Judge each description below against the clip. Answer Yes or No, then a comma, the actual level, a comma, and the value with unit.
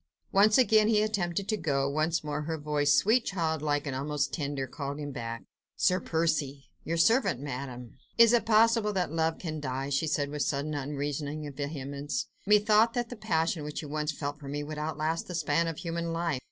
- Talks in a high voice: No, medium, 155 Hz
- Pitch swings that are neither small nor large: Yes, average, 3.6 semitones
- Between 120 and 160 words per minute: No, average, 190 wpm